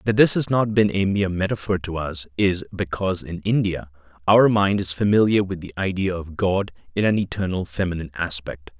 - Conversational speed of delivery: Yes, average, 190 wpm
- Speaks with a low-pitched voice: Yes, very low, 95 Hz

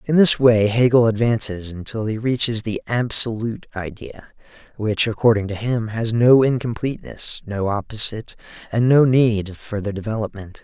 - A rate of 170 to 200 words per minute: No, average, 145 wpm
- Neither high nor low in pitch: No, low, 110 Hz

